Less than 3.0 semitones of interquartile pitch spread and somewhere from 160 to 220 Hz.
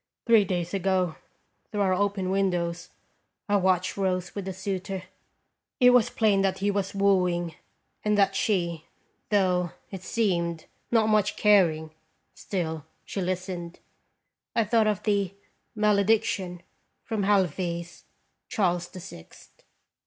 Yes: narrow, 2.5 semitones; high, 190 Hz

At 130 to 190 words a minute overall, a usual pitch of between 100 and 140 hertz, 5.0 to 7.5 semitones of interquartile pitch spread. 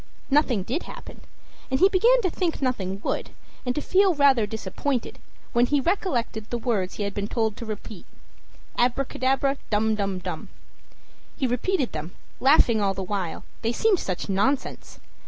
No: average, 160 wpm; high, 240 Hz; wide, 5.6 semitones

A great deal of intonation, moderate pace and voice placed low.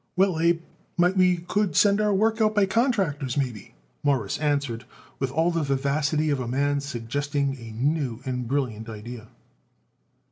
No: wide, 5.7 semitones; average, 155 wpm; medium, 145 Hz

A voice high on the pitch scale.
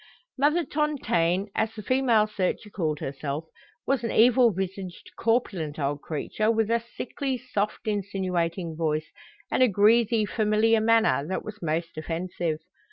Yes: high, 205 Hz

